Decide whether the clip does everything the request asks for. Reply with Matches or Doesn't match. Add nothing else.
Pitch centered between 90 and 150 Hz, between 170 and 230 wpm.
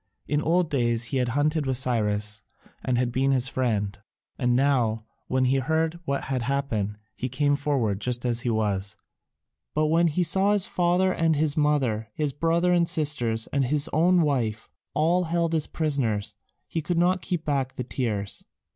Matches